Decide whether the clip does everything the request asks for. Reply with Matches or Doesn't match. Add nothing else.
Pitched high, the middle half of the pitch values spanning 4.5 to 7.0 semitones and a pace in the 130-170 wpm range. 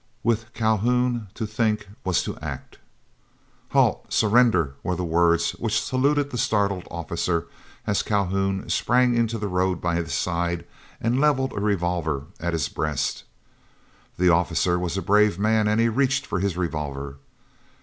Doesn't match